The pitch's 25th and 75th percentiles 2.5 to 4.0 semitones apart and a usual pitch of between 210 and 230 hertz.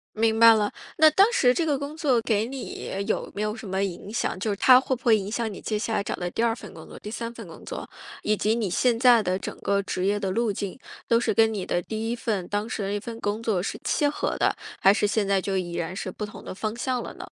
Yes: average, 2.8 semitones; high, 220 Hz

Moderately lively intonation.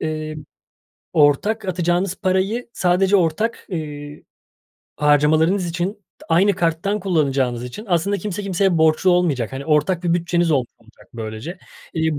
Yes: average, 4.0 semitones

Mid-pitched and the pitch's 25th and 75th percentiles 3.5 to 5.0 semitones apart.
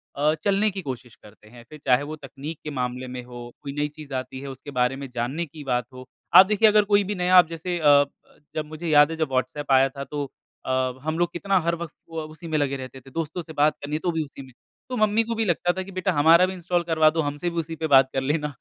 Yes: medium, 150 Hz; average, 4.2 semitones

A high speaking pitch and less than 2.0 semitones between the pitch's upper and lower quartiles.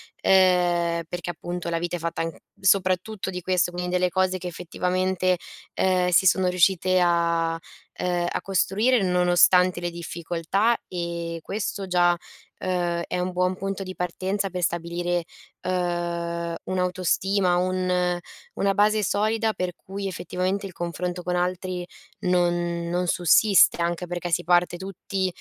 No: medium, 180 Hz; narrow, 1.2 semitones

